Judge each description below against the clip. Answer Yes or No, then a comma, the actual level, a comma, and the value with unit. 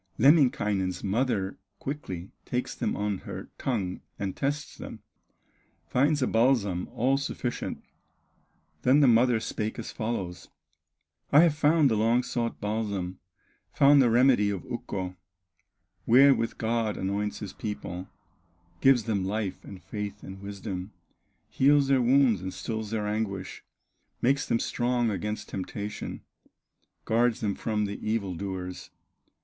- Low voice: Yes, low, 110 Hz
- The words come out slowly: Yes, slow, 130 wpm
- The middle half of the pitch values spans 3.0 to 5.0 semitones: Yes, average, 4.1 semitones